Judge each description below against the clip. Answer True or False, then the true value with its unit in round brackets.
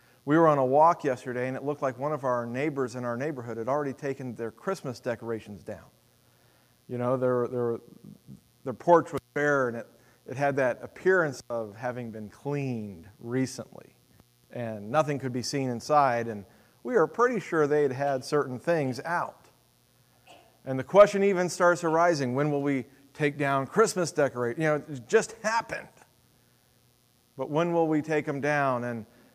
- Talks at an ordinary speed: True (175 wpm)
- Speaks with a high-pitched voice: False (135 Hz)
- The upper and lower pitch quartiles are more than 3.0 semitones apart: True (4.0 semitones)